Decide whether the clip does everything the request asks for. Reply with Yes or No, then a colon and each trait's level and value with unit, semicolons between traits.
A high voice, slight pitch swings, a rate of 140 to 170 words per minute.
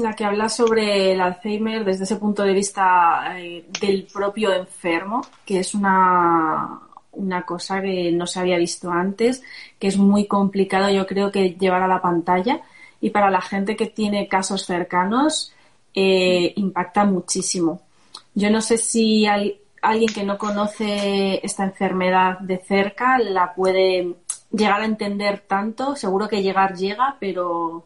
Yes: high, 195 Hz; narrow, 2.1 semitones; average, 155 wpm